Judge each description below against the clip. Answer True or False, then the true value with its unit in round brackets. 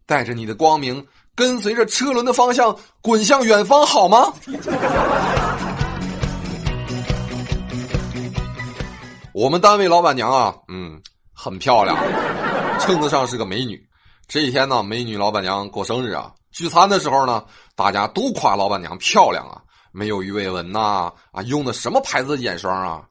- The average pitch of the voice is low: True (120 Hz)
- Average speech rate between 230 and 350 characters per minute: False (220 characters per minute)